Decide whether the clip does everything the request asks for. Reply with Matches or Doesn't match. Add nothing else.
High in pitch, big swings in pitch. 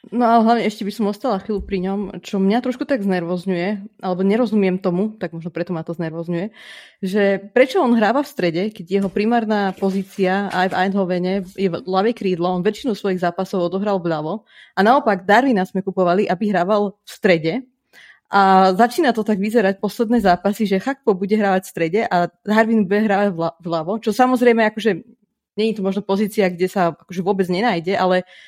Doesn't match